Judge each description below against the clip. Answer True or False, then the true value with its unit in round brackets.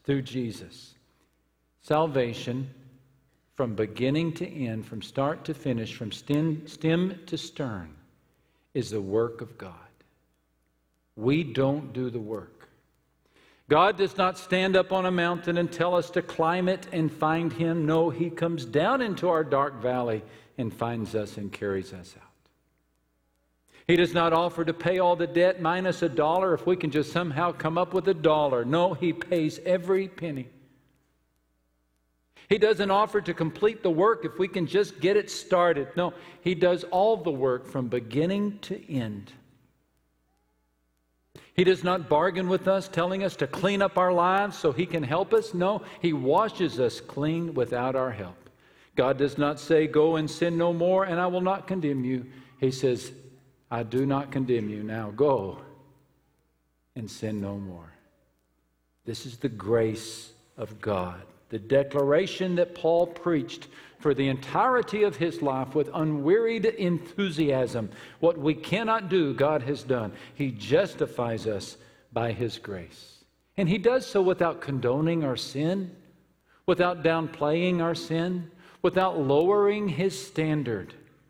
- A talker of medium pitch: True (150 Hz)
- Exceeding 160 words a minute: False (155 wpm)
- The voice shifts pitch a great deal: True (6.9 semitones)